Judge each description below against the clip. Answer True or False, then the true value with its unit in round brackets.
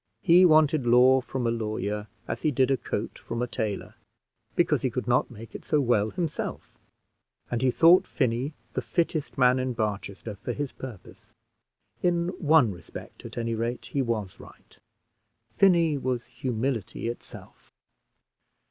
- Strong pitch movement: False (4.3 semitones)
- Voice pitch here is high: False (125 Hz)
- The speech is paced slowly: False (155 wpm)